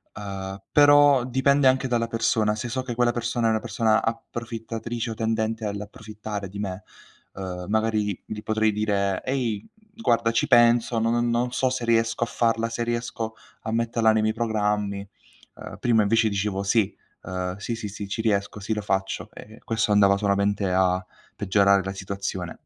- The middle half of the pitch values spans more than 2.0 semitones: Yes, narrow, 2.6 semitones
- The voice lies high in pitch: No, low, 110 Hz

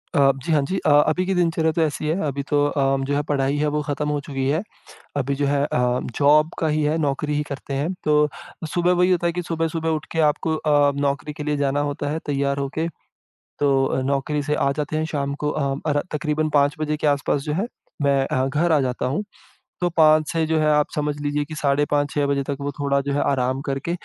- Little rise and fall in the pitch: Yes, narrow, 1.8 semitones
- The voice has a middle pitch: Yes, medium, 145 Hz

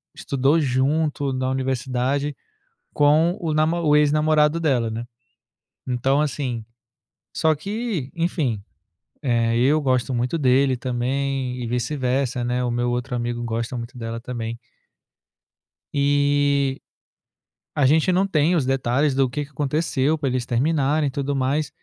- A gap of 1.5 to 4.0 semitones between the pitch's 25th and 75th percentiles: Yes, average, 3.2 semitones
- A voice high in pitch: No, low, 135 Hz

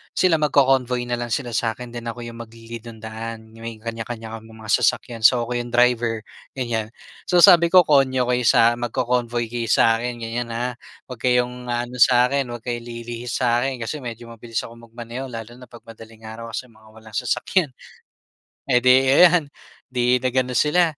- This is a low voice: Yes, low, 120 Hz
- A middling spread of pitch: No, narrow, 1.6 semitones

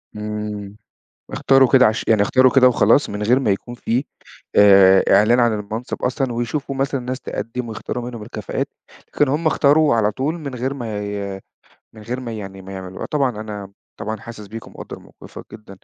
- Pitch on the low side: Yes, low, 115 Hz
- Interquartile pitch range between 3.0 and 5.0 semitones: Yes, average, 3.7 semitones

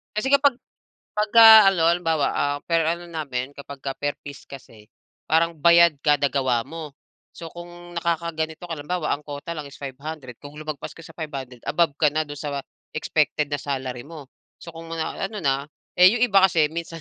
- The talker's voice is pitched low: No, medium, 155 Hz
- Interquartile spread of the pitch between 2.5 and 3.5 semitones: Yes, average, 3.1 semitones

